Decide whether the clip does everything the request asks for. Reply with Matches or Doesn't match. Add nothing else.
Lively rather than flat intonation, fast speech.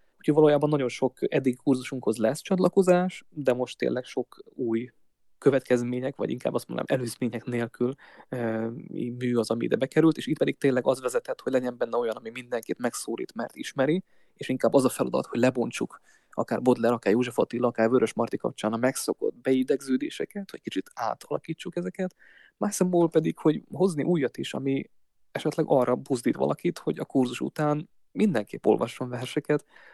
Matches